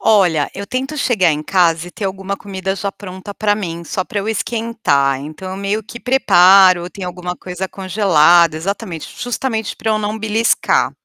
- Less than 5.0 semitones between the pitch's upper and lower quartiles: Yes, average, 3.4 semitones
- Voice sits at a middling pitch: No, high, 195 Hz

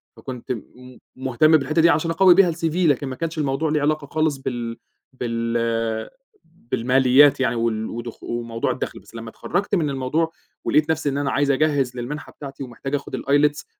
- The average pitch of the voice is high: No, low, 135 Hz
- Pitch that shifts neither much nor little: Yes, average, 4.3 semitones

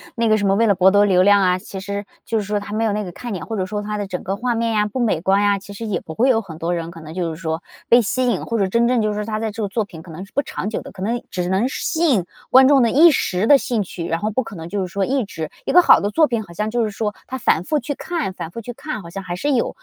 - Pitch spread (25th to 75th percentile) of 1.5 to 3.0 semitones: No, average, 3.7 semitones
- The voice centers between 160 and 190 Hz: No, high, 205 Hz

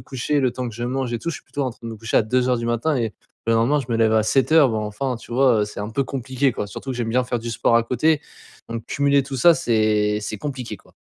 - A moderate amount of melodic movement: Yes, average, 3.1 semitones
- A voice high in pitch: No, low, 120 Hz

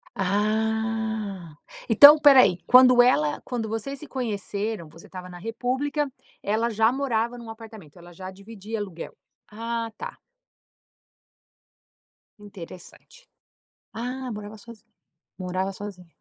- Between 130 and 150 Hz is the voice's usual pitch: No, high, 220 Hz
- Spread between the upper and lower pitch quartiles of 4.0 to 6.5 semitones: No, average, 3.6 semitones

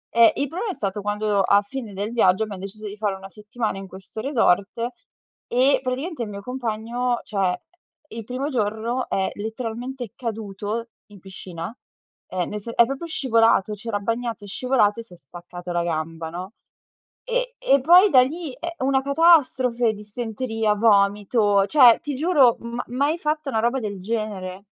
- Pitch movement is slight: No, average, 4.3 semitones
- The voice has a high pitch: Yes, high, 225 Hz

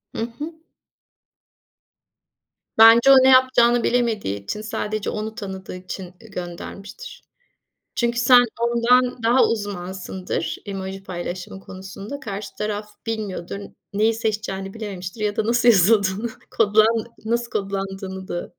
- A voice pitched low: No, high, 210 Hz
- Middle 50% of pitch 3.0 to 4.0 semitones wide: Yes, average, 3.5 semitones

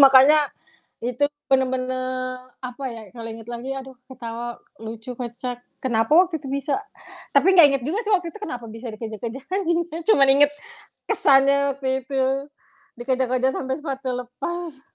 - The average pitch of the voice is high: Yes, very high, 260 Hz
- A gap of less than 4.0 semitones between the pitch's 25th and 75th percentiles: Yes, narrow, 2.4 semitones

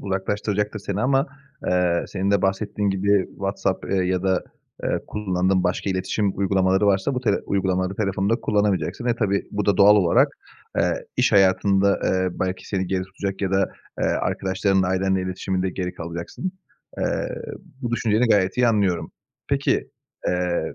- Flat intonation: Yes, narrow, 1.7 semitones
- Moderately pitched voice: No, very low, 95 Hz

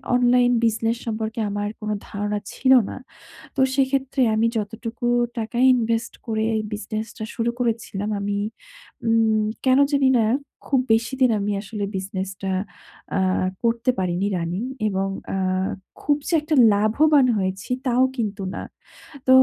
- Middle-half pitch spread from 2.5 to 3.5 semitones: Yes, average, 3.1 semitones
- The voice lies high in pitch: Yes, high, 225 Hz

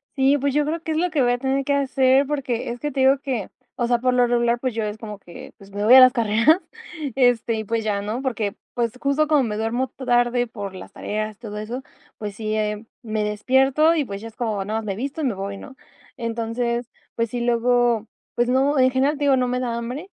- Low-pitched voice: No, high, 240 Hz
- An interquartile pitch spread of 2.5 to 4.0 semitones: Yes, average, 3.4 semitones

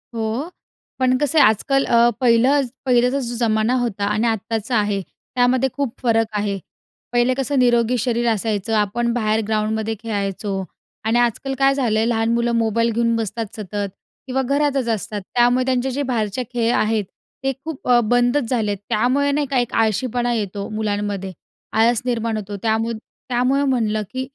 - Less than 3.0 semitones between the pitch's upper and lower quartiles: Yes, narrow, 2.6 semitones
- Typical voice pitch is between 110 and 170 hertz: No, high, 235 Hz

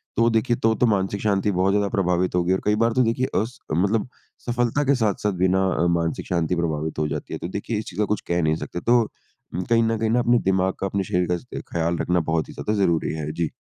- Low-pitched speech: Yes, very low, 95 Hz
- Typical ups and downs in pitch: Yes, average, 4.6 semitones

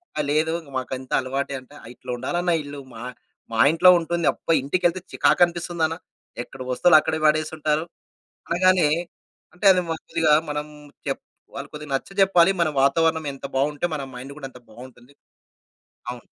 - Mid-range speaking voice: Yes, medium, 155 Hz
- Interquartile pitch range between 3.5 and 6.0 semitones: Yes, average, 3.9 semitones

